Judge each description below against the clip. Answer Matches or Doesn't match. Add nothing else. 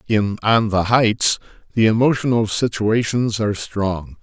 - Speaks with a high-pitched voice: Doesn't match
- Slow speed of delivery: Matches